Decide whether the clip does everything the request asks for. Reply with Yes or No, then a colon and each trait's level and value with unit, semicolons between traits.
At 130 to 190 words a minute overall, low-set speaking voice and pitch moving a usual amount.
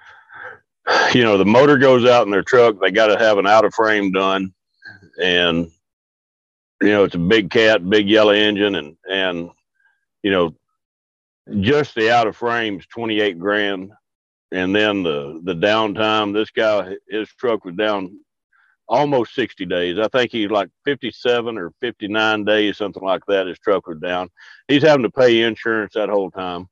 Yes: average, 175 wpm; low, 105 Hz; average, 3.3 semitones